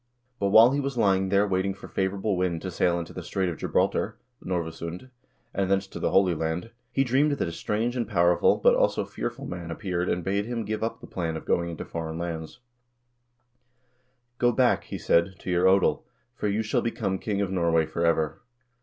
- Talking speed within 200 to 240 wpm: Yes, fast, 205 wpm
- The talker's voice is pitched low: Yes, very low, 95 Hz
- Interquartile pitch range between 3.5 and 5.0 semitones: Yes, average, 4.0 semitones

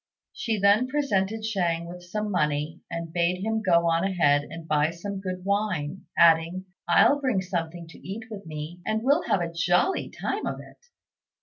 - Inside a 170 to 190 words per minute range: Yes, average, 180 wpm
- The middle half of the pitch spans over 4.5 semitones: No, average, 3.8 semitones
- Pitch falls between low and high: Yes, medium, 180 Hz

